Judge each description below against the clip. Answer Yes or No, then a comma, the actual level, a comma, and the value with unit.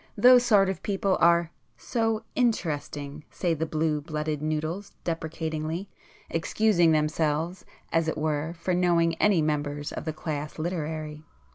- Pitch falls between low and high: Yes, medium, 160 Hz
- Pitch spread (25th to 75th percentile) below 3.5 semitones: Yes, average, 2.9 semitones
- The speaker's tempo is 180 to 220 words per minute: No, slow, 135 wpm